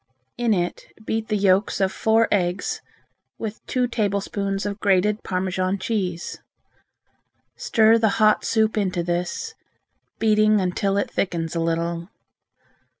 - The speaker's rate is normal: No, slow, 125 wpm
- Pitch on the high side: Yes, high, 200 Hz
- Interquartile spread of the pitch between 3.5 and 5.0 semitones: No, average, 3.1 semitones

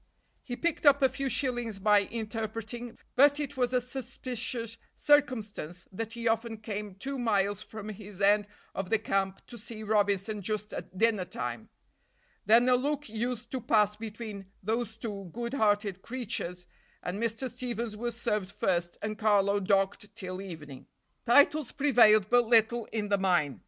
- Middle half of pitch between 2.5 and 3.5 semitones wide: Yes, average, 3.1 semitones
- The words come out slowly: No, average, 160 wpm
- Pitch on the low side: No, high, 220 Hz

